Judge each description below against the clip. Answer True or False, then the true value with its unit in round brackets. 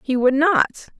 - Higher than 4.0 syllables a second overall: True (5.1 syllables/s)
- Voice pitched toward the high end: True (280 Hz)